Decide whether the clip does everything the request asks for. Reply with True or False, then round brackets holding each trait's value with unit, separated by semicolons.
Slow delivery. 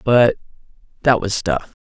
True (130 wpm)